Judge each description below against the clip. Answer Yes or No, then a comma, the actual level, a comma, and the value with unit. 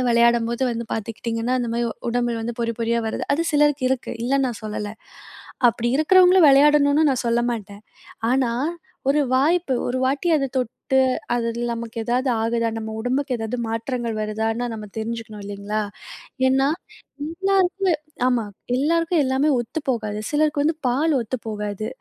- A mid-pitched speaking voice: No, high, 240 Hz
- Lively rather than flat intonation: No, average, 4.0 semitones